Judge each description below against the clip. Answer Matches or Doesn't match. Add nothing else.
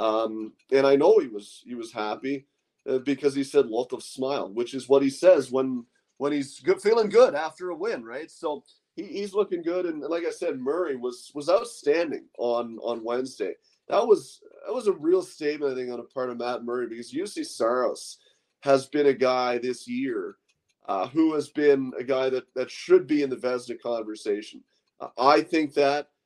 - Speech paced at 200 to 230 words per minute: Matches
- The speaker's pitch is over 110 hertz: Matches